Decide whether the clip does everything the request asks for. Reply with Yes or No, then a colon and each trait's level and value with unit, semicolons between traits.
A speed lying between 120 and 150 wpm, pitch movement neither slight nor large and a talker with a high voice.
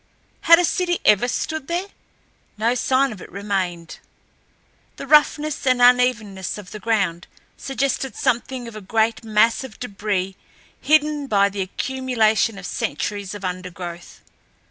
Yes: average, 140 wpm; average, 4.9 semitones; high, 225 Hz